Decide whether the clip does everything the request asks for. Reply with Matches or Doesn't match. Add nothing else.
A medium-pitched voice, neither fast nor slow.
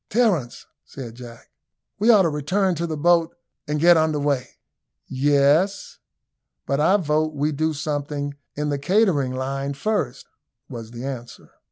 Matches